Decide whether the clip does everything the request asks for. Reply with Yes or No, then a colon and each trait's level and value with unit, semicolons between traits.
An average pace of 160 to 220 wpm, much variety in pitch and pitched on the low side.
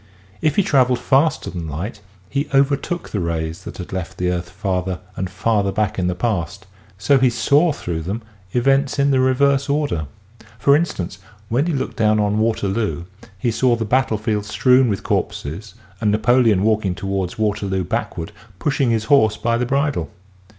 Yes: average, 175 wpm; wide, 5.7 semitones; low, 110 Hz